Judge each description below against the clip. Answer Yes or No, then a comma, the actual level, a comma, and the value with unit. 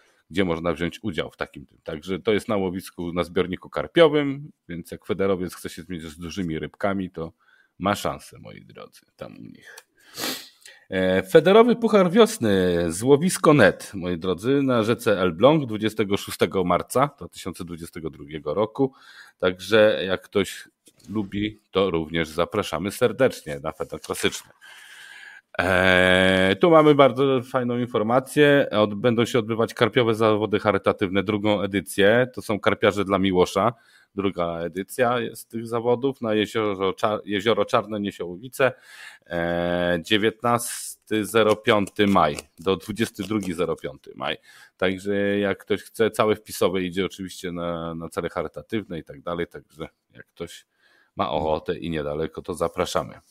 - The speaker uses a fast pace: No, average, 135 wpm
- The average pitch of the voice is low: Yes, low, 100 Hz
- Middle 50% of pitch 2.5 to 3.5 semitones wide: No, average, 4.2 semitones